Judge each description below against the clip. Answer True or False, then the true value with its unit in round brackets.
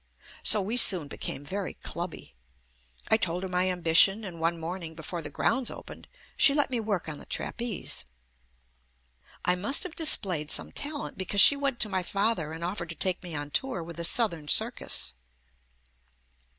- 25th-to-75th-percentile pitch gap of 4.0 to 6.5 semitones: True (5.0 semitones)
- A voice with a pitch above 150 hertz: True (185 Hz)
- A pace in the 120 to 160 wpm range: False (175 wpm)